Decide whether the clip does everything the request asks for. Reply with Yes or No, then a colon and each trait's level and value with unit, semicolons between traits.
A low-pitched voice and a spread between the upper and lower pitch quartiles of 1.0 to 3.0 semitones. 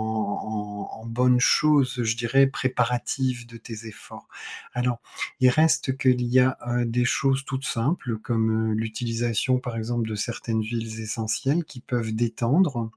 Yes: low, 120 Hz; narrow, 2.4 semitones